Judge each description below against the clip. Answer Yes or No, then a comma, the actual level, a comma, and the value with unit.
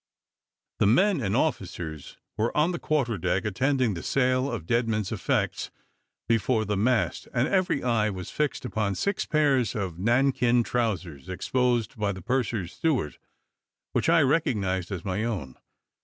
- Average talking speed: Yes, average, 155 wpm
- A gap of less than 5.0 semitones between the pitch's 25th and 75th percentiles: No, average, 5.3 semitones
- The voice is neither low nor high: No, low, 115 Hz